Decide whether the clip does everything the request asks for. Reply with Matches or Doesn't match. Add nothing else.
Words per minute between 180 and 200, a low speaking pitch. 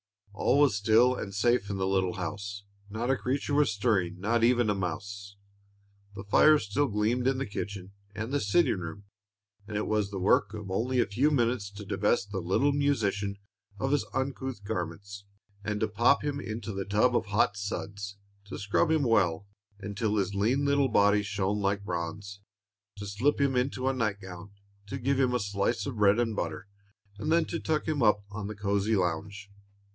Matches